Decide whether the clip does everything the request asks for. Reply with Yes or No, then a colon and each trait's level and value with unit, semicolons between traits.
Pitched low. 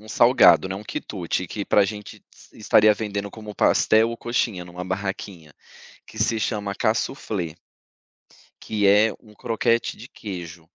Yes: low, 105 Hz